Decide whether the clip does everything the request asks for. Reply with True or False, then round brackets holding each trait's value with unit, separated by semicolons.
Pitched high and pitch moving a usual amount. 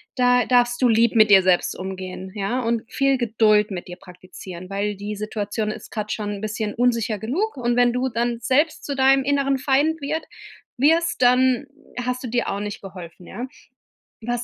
True (235 Hz; 3.8 semitones)